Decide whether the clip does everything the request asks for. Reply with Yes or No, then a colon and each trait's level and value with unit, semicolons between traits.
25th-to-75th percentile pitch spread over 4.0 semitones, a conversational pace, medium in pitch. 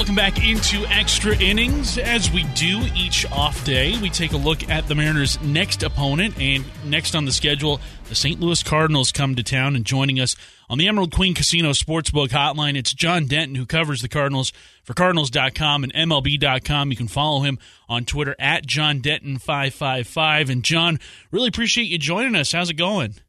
No: average, 3.3 semitones; average, 185 wpm; medium, 145 Hz